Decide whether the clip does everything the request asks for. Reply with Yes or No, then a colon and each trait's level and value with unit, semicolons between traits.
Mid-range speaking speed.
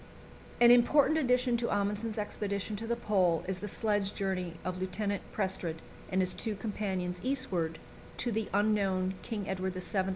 Yes: average, 160 wpm